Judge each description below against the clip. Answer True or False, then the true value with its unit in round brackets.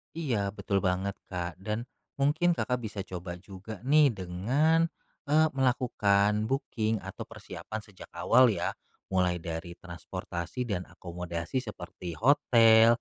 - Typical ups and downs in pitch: False (5.9 semitones)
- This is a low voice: True (105 Hz)